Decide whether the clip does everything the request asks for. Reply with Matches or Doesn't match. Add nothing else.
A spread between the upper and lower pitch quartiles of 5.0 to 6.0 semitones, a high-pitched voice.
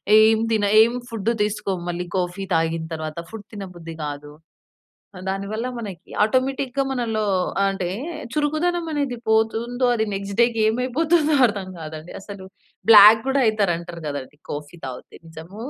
Matches